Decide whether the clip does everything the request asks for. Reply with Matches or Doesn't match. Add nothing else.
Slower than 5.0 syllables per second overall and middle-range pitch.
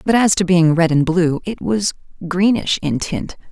Matches